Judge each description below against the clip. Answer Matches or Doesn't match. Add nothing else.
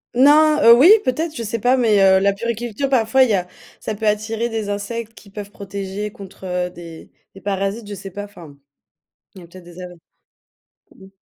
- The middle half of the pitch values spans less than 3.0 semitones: Doesn't match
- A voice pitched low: Doesn't match